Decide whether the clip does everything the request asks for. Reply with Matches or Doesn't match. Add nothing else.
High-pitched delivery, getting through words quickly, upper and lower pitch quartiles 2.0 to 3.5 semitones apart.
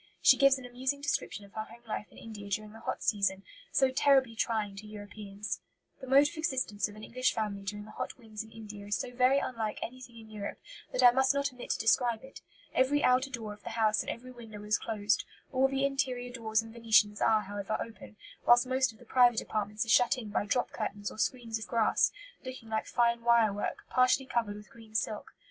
Matches